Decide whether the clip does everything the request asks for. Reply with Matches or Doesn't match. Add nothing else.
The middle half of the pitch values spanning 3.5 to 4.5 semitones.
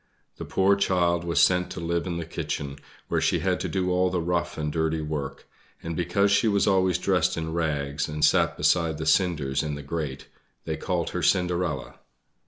Doesn't match